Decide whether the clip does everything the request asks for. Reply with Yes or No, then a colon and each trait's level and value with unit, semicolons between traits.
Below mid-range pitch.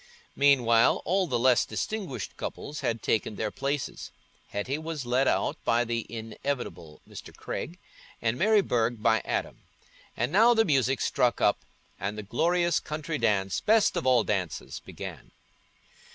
Yes: low, 125 Hz